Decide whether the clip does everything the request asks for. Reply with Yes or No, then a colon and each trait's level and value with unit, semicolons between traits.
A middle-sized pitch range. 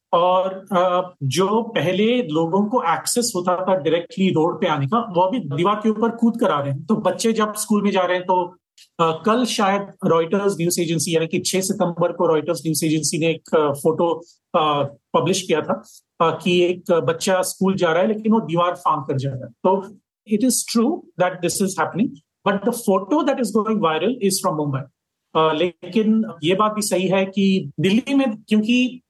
Yes: average, 4.4 semitones